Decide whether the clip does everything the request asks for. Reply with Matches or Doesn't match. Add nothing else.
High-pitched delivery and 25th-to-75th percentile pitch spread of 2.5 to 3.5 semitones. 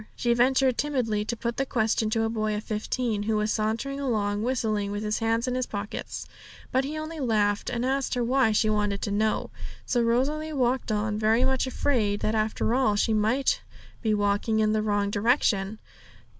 Matches